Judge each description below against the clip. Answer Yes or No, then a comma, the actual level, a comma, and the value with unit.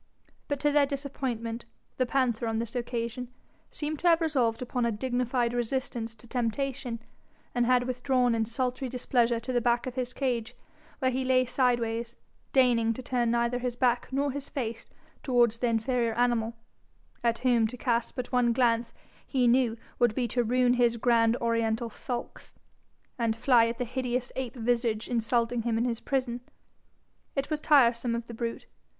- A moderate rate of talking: Yes, average, 170 wpm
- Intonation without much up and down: Yes, narrow, 1.7 semitones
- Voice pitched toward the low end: No, high, 245 Hz